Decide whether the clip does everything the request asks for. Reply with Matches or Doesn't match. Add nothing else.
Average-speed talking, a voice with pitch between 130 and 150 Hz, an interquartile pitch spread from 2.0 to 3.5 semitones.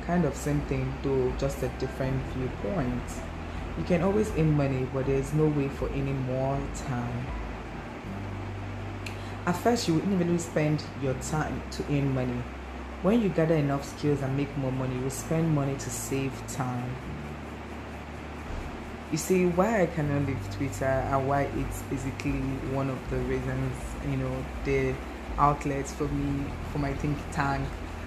Doesn't match